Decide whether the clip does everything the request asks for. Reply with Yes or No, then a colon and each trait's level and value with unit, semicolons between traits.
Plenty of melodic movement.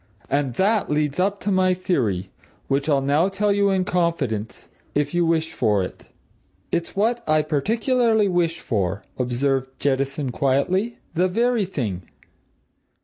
Yes: wide, 6.2 semitones